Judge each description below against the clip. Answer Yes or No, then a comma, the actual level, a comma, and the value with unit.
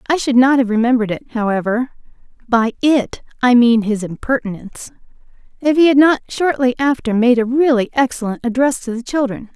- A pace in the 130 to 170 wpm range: Yes, average, 165 wpm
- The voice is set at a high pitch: Yes, high, 245 Hz